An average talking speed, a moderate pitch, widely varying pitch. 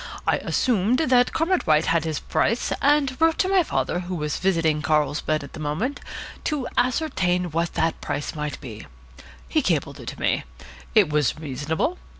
Yes: average, 170 wpm; medium, 175 Hz; wide, 9.0 semitones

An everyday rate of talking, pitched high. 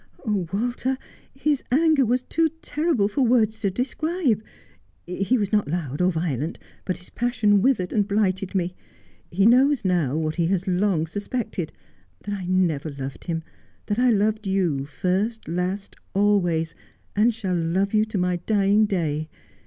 Yes: average, 160 wpm; high, 195 Hz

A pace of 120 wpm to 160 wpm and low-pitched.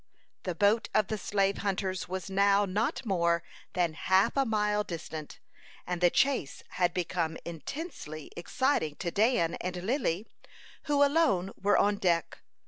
No: average, 145 wpm; high, 190 Hz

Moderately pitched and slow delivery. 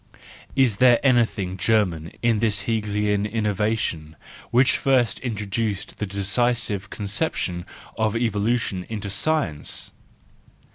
No: low, 105 Hz; slow, 100 wpm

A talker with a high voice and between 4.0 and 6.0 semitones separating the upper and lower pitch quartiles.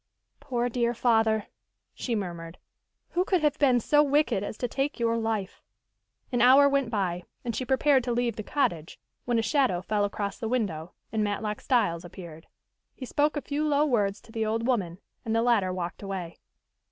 Yes: high, 230 Hz; average, 4.7 semitones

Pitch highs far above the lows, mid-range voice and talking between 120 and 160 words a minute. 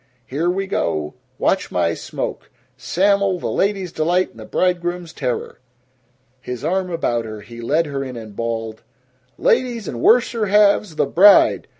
Yes: wide, 8.7 semitones; medium, 170 Hz; average, 155 wpm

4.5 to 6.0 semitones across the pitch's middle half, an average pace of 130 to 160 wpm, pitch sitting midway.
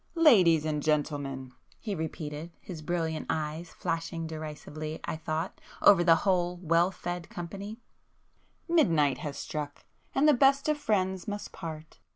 No: average, 3.5 semitones; average, 140 wpm; medium, 165 Hz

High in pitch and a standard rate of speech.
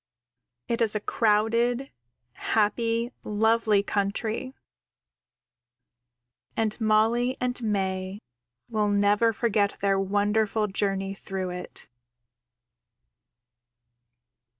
No: high, 215 Hz; slow, 80 wpm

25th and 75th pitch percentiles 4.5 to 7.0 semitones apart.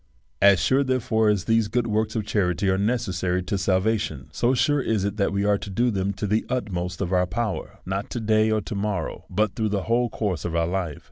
No: average, 2.9 semitones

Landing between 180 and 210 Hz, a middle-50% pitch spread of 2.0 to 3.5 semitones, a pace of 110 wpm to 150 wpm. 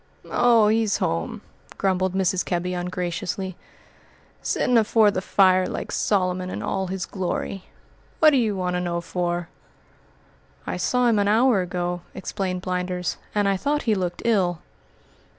Yes: medium, 185 Hz; average, 2.7 semitones; average, 145 wpm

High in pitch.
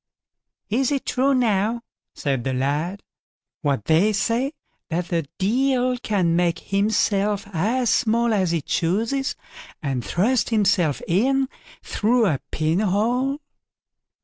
Yes: high, 205 Hz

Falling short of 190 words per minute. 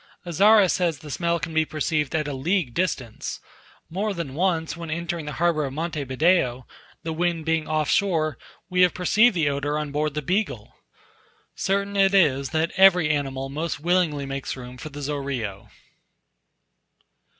Yes: average, 165 wpm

